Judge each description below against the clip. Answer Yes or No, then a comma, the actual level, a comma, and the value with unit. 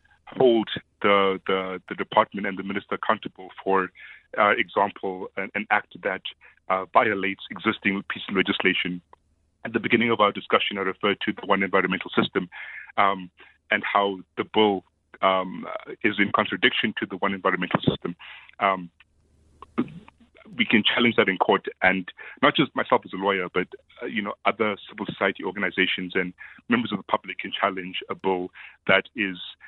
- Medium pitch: No, very low, 95 Hz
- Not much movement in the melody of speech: Yes, narrow, 1.3 semitones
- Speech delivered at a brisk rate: No, average, 165 wpm